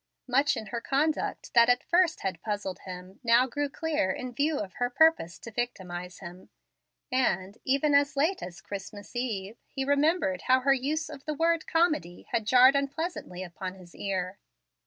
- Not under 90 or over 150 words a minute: No, average, 175 wpm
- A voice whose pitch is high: Yes, high, 245 Hz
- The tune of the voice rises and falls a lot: Yes, wide, 7.1 semitones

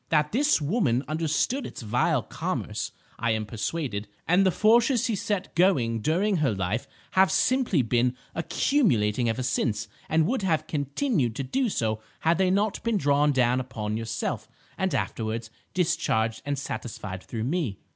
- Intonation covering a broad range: Yes, wide, 8.8 semitones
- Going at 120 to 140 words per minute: No, average, 155 wpm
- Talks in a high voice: No, medium, 145 Hz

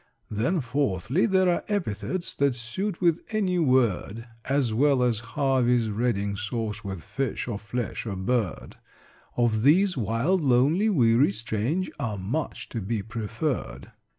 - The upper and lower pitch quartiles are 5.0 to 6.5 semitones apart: Yes, wide, 5.5 semitones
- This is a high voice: No, low, 120 Hz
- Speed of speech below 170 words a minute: Yes, average, 140 wpm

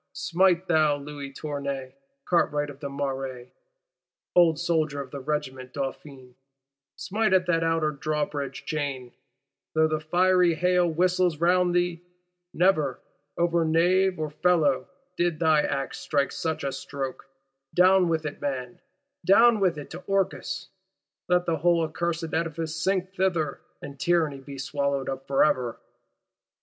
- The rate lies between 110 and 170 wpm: Yes, average, 140 wpm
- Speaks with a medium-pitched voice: Yes, medium, 155 Hz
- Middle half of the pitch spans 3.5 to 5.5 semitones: Yes, average, 3.9 semitones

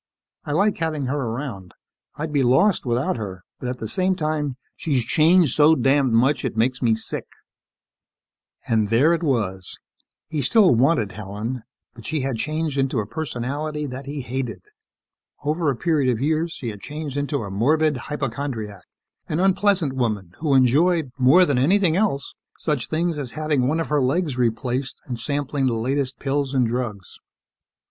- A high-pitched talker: No, low, 135 Hz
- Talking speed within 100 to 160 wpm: No, average, 170 wpm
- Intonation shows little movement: No, average, 4.4 semitones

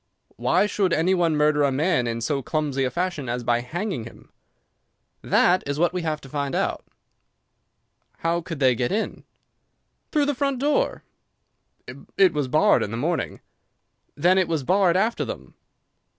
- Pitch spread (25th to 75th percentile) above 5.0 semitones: Yes, wide, 5.4 semitones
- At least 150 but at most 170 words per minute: Yes, average, 165 wpm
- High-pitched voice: No, medium, 160 Hz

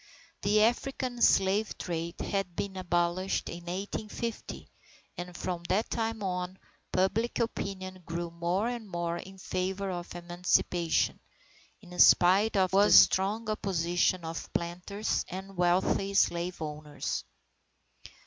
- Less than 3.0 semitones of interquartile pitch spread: Yes, narrow, 2.5 semitones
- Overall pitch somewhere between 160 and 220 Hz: Yes, medium, 185 Hz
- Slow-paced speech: Yes, slow, 120 wpm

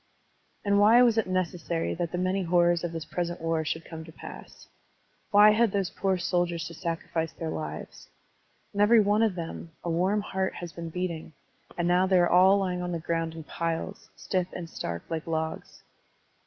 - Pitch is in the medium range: Yes, medium, 175 Hz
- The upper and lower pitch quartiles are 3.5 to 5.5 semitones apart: No, narrow, 2.5 semitones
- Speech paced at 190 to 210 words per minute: Yes, average, 195 wpm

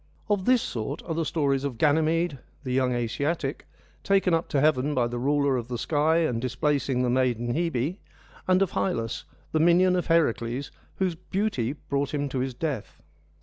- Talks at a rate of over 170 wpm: Yes, average, 180 wpm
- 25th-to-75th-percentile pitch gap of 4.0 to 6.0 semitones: Yes, average, 4.7 semitones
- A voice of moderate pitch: Yes, medium, 145 Hz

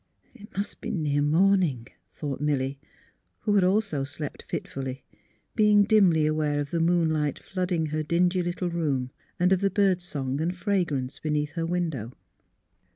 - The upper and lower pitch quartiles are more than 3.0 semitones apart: Yes, average, 3.9 semitones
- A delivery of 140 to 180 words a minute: Yes, average, 155 wpm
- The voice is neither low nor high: Yes, medium, 165 Hz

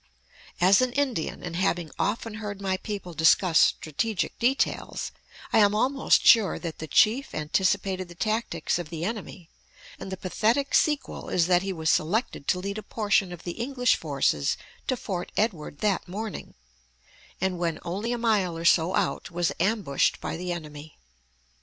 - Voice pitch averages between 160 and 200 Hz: Yes, high, 190 Hz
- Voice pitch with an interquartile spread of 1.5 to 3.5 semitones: No, average, 4.4 semitones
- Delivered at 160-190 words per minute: Yes, average, 165 wpm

